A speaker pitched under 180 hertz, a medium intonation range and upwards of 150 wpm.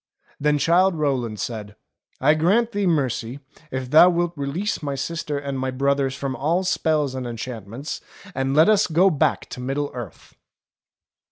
Yes: medium, 140 Hz; average, 4.2 semitones; average, 160 wpm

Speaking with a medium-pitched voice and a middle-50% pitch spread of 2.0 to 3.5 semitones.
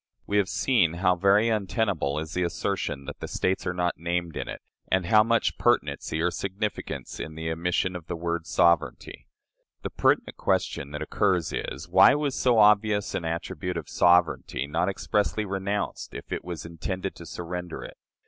No: very low, 90 Hz; average, 3.2 semitones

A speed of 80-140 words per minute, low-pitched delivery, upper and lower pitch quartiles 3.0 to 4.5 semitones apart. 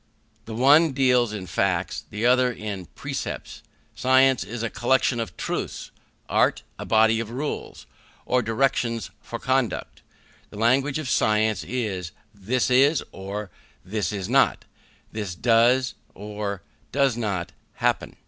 Yes: slow, 135 wpm; low, 115 Hz; average, 3.5 semitones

